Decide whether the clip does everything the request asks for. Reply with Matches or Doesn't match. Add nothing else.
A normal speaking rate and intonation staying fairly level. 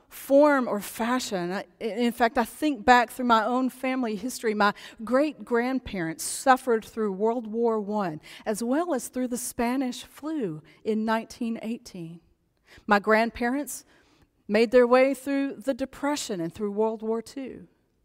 Doesn't match